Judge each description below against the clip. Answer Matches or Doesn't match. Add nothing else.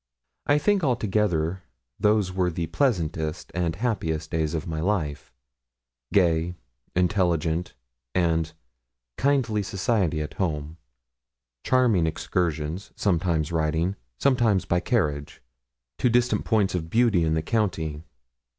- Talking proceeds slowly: Matches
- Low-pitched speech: Matches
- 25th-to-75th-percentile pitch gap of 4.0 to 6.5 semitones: Matches